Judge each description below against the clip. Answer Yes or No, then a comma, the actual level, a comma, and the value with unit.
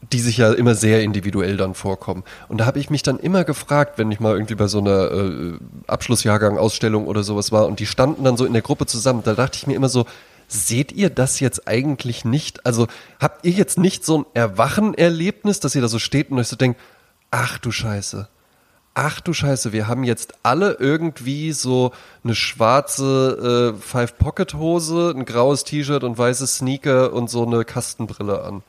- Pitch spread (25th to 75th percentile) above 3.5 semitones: Yes, average, 4.4 semitones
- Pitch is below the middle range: Yes, low, 120 Hz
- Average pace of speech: No, fast, 195 wpm